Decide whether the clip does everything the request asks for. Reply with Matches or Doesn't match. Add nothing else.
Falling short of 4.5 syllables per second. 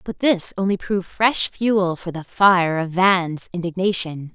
Matches